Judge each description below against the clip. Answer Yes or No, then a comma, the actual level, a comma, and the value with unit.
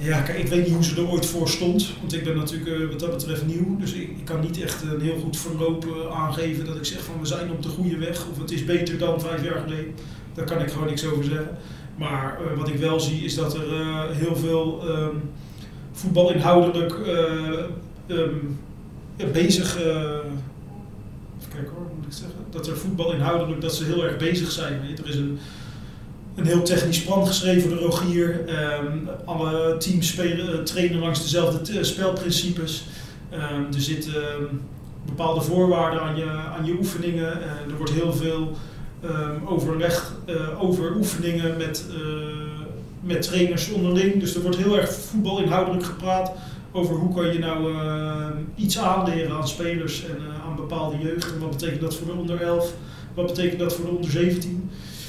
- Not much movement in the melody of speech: Yes, narrow, 1.8 semitones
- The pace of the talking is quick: No, average, 185 wpm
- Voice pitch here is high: No, medium, 165 Hz